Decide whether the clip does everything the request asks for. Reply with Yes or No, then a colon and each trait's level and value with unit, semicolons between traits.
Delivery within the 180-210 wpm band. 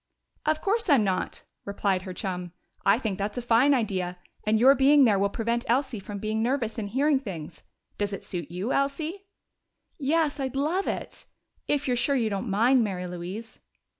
Yes: average, 190 wpm